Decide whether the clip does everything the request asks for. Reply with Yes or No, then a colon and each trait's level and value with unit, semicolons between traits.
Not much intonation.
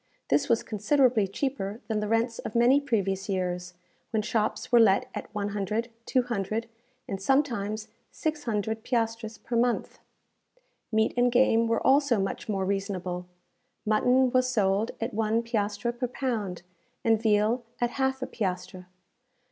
No: average, 3.3 semitones